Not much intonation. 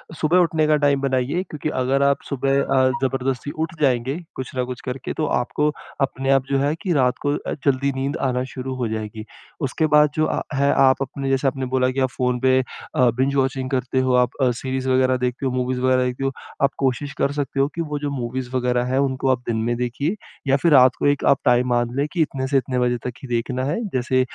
Yes: narrow, 1.7 semitones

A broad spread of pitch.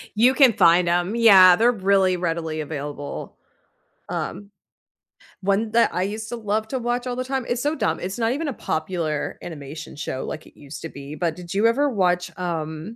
Yes: wide, 6.1 semitones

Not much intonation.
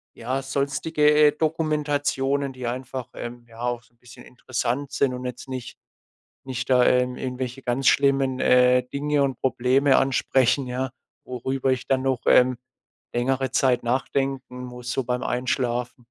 Yes: narrow, 1.6 semitones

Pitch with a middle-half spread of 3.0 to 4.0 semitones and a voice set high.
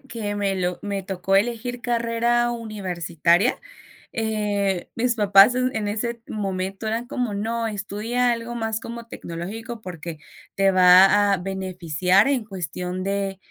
Yes: average, 3.5 semitones; high, 205 Hz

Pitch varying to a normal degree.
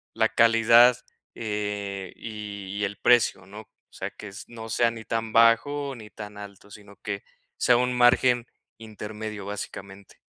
No: narrow, 2.2 semitones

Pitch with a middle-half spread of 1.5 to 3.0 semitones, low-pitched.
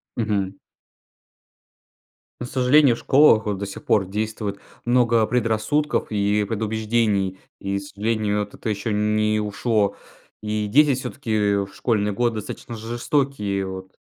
Yes: narrow, 2.6 semitones; low, 105 Hz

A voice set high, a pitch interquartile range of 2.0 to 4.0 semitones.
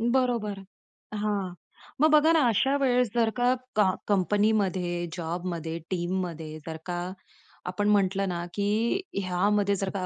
Yes: high, 195 Hz; average, 3.5 semitones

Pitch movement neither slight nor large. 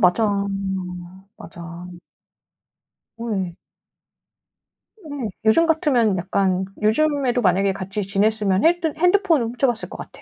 No: wide, 7.0 semitones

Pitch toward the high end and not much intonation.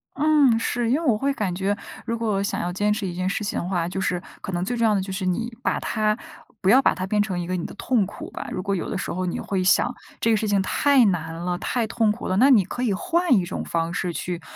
No: high, 200 Hz; average, 4.1 semitones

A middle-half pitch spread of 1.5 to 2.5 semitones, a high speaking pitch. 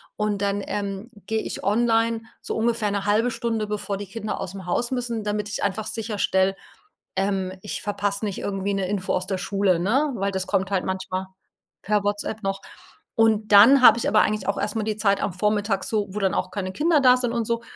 Yes: narrow, 2.2 semitones; high, 205 Hz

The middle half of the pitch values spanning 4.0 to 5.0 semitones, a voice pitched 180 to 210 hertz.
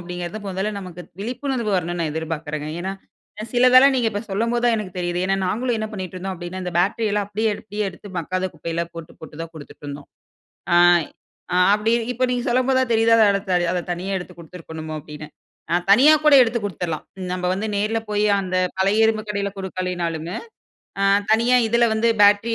Yes: average, 4.3 semitones; high, 195 Hz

